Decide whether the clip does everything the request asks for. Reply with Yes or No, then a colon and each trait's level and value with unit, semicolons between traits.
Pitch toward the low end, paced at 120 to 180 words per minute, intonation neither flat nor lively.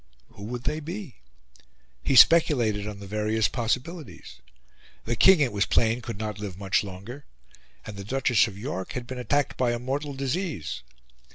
Yes: low, 120 Hz; average, 170 wpm; average, 4.9 semitones